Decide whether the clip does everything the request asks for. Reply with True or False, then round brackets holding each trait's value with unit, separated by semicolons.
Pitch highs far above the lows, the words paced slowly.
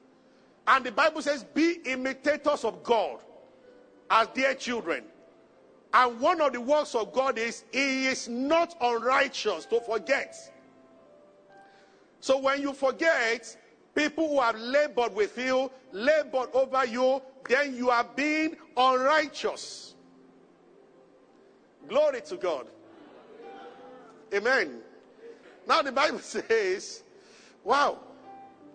False (3.4 semitones; 110 wpm)